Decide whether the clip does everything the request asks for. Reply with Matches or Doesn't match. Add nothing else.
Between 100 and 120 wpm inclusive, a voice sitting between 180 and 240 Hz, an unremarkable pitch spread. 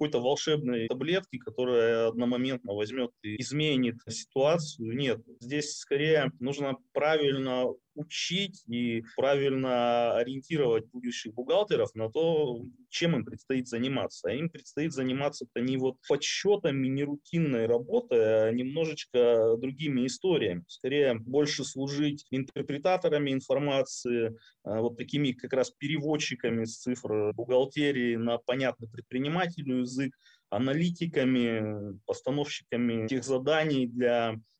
Doesn't match